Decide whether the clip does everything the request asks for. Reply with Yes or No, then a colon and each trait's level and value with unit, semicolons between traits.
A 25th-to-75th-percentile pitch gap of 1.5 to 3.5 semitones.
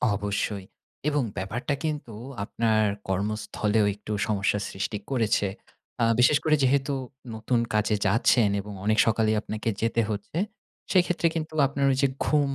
No: average, 4.8 semitones